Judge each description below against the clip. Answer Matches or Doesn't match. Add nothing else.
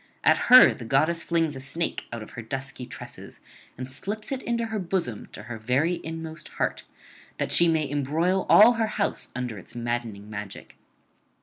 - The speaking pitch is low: Doesn't match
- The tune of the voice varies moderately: Doesn't match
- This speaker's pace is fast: Doesn't match